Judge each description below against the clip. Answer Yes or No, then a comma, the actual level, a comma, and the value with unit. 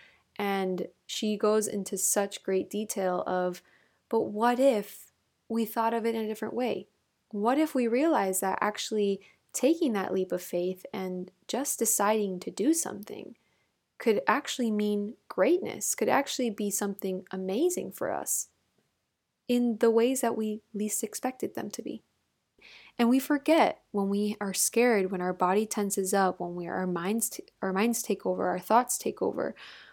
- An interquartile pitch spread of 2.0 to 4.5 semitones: Yes, average, 3.4 semitones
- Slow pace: No, average, 165 wpm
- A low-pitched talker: No, high, 210 Hz